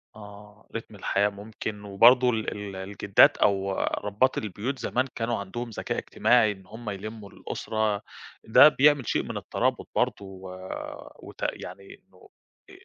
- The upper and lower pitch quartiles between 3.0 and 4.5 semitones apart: No, narrow, 2.4 semitones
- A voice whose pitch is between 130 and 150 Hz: No, low, 105 Hz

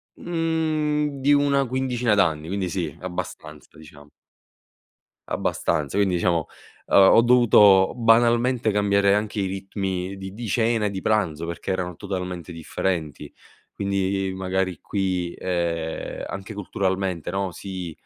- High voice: No, very low, 95 Hz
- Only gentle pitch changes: No, average, 4.0 semitones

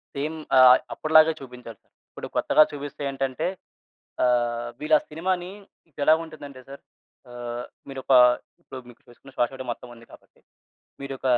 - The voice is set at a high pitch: No, low, 135 Hz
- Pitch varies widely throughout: No, average, 3.8 semitones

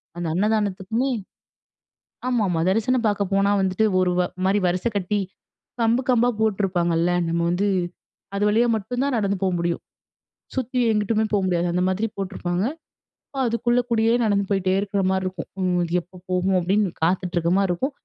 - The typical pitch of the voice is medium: No, high, 195 Hz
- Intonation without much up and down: No, average, 3.5 semitones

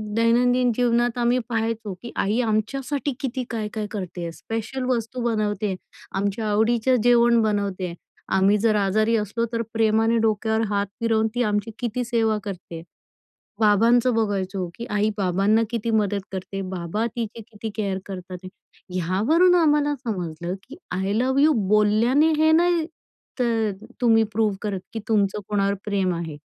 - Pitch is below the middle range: No, high, 220 Hz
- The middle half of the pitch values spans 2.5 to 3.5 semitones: Yes, average, 2.9 semitones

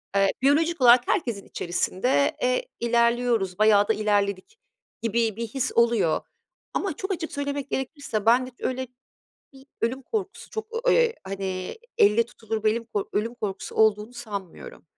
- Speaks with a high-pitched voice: Yes, high, 235 Hz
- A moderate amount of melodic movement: Yes, average, 4.3 semitones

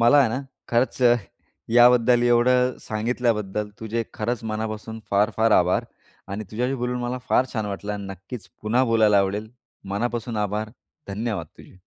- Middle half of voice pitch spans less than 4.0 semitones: Yes, narrow, 2.4 semitones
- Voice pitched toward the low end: Yes, low, 110 Hz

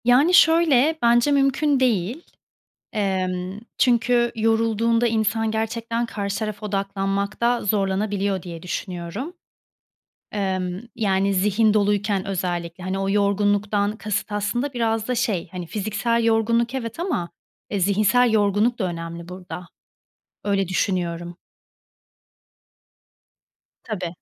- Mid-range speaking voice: No, high, 210 Hz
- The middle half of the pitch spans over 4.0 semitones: No, average, 3.4 semitones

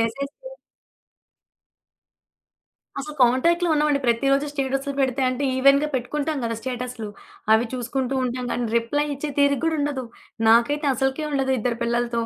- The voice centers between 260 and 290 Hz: Yes, very high, 270 Hz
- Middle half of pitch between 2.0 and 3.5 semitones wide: Yes, average, 2.9 semitones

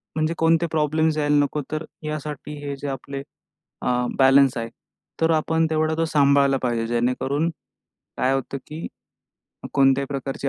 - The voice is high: No, medium, 145 Hz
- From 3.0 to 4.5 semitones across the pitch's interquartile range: No, narrow, 2.5 semitones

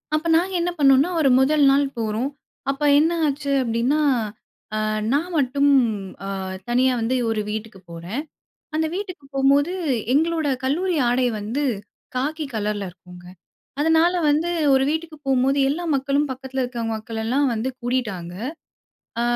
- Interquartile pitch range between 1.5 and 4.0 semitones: No, average, 4.7 semitones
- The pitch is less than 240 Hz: No, very high, 270 Hz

